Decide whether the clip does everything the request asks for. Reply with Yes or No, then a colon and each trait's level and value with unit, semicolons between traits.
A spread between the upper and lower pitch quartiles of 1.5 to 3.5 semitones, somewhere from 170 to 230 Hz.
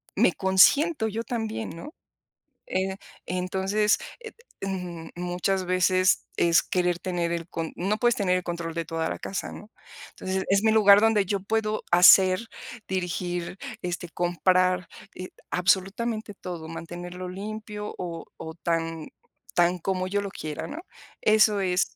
Yes: average, 2.8 semitones; medium, 185 Hz